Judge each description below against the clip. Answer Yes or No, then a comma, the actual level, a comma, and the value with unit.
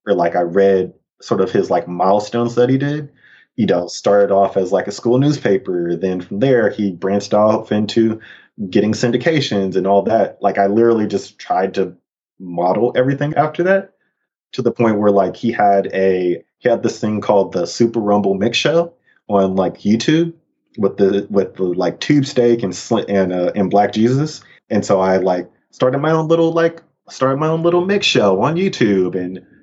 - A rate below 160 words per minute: No, average, 195 wpm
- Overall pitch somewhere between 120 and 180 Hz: No, low, 105 Hz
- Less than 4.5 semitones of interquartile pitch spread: No, wide, 5.6 semitones